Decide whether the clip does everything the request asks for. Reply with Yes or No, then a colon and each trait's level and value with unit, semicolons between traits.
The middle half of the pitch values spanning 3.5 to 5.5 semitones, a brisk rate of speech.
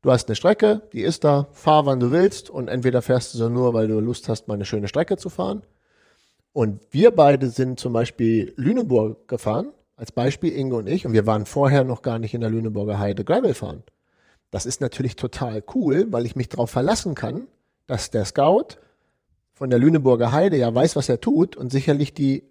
Yes: average, 4.1 semitones; fast, 210 wpm